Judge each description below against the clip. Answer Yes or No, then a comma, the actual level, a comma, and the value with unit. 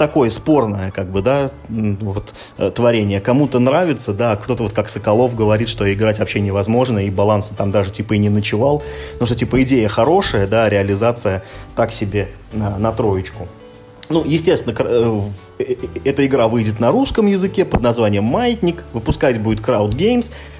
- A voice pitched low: Yes, low, 110 Hz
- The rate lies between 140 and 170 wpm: Yes, average, 155 wpm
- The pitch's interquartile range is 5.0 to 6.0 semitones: No, average, 4.0 semitones